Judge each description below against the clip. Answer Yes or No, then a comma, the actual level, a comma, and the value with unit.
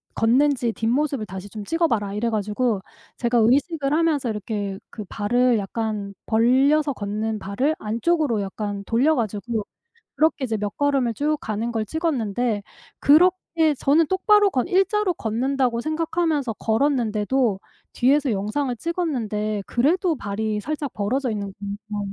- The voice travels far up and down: Yes, wide, 5.8 semitones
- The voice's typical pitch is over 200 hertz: Yes, high, 240 Hz